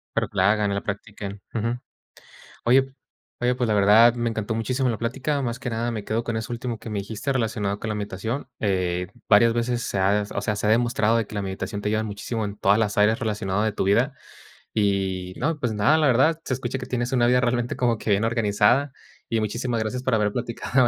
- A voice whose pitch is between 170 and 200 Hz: No, low, 110 Hz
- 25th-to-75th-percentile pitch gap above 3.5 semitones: No, average, 2.9 semitones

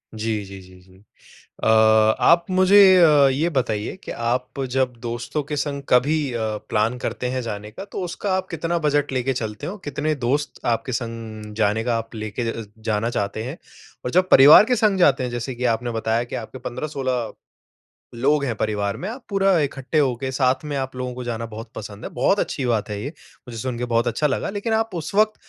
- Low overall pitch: Yes, low, 125 Hz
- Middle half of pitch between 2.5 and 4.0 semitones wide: No, average, 5.1 semitones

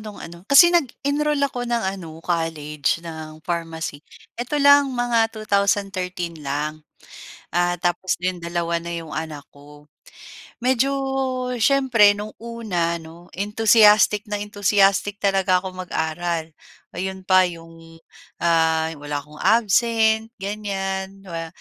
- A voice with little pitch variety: No, average, 4.5 semitones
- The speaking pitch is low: No, medium, 185 Hz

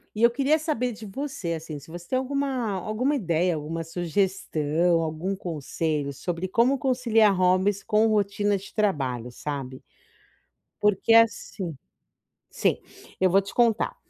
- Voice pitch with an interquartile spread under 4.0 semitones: No, wide, 5.6 semitones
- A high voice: Yes, high, 195 Hz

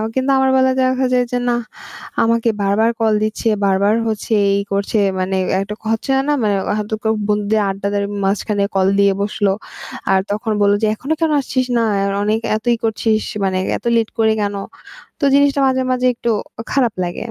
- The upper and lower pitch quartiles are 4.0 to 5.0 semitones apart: No, average, 3.5 semitones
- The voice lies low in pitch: No, high, 220 Hz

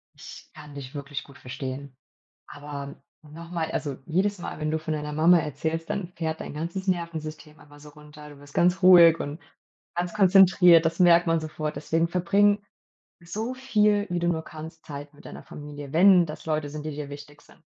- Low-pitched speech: No, medium, 160 Hz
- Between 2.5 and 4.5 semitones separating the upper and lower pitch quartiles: Yes, average, 2.8 semitones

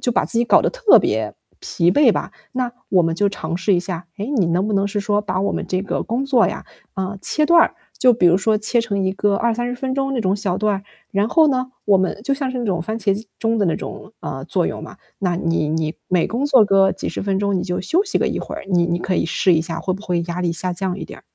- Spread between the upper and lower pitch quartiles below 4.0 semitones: No, average, 4.7 semitones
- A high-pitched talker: Yes, high, 200 Hz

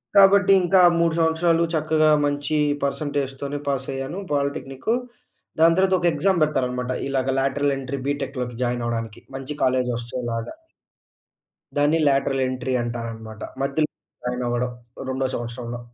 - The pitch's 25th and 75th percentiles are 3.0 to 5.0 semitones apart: Yes, average, 3.6 semitones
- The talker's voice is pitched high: No, low, 135 Hz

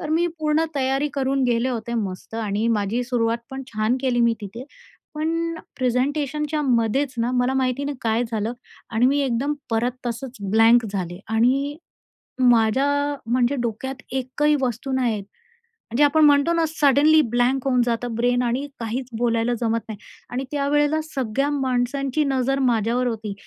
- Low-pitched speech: No, very high, 250 Hz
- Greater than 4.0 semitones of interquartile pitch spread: No, average, 3.4 semitones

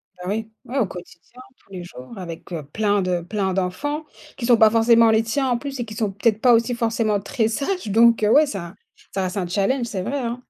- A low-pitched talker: No, high, 220 Hz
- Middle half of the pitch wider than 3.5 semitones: Yes, average, 3.9 semitones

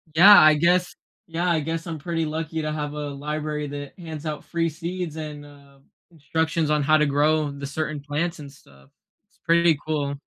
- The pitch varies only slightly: Yes, narrow, 2.0 semitones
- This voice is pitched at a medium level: Yes, medium, 155 Hz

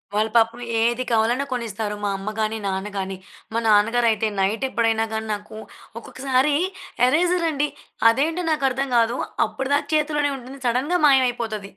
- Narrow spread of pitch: No, average, 3.9 semitones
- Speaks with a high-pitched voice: Yes, high, 235 Hz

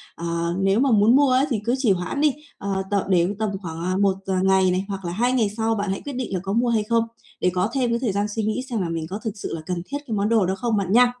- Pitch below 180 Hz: No, high, 205 Hz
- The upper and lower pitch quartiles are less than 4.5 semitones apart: Yes, average, 4.0 semitones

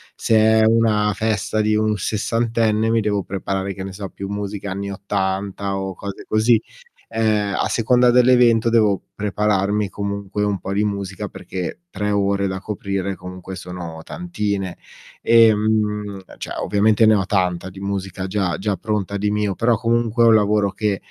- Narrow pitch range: Yes, narrow, 2.0 semitones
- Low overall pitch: Yes, low, 105 Hz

